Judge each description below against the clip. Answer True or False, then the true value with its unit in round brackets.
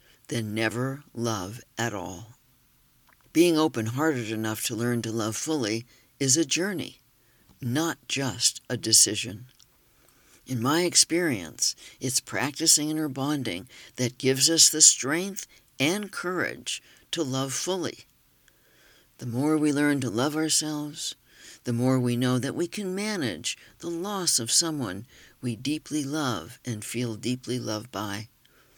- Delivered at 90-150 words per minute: True (135 wpm)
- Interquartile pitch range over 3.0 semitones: True (4.7 semitones)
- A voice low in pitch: True (130 Hz)